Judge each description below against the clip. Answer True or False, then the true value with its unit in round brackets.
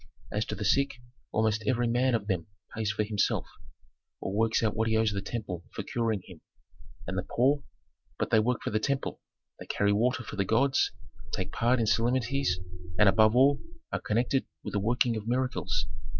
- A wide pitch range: False (3.1 semitones)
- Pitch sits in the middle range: False (110 Hz)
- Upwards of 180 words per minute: True (195 wpm)